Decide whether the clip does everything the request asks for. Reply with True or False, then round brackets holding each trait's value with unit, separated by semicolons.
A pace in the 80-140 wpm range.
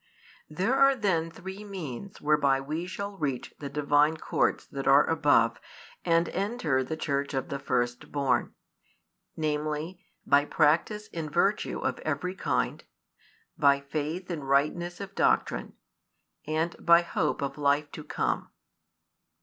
True (135 wpm)